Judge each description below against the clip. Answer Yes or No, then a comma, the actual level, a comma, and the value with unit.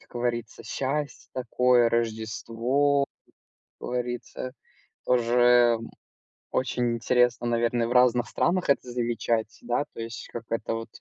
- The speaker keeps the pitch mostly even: Yes, narrow, 1.3 semitones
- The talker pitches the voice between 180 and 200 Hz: No, low, 120 Hz